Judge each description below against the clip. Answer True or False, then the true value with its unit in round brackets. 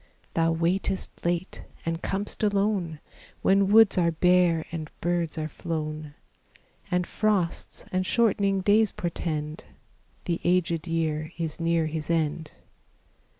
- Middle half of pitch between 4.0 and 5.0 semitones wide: False (2.9 semitones)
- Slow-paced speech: True (120 wpm)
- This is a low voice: False (170 Hz)